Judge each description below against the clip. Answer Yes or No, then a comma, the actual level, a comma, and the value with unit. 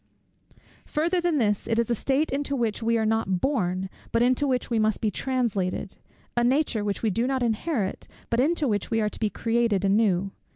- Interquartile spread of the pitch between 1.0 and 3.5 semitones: No, average, 4.1 semitones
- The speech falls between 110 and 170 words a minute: No, fast, 205 wpm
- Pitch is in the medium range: No, high, 230 Hz